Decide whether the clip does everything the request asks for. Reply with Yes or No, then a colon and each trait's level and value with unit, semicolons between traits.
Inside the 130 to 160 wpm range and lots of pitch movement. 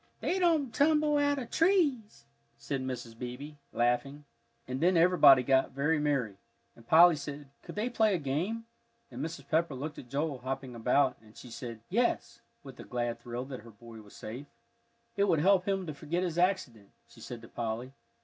No: average, 190 wpm; wide, 6.9 semitones